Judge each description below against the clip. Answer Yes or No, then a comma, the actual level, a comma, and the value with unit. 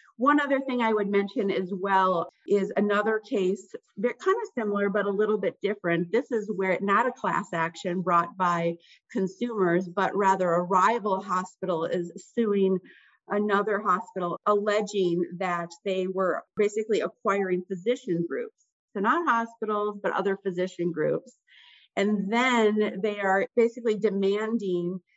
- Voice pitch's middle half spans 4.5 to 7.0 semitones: No, average, 2.9 semitones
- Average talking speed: Yes, average, 145 wpm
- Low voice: No, high, 200 Hz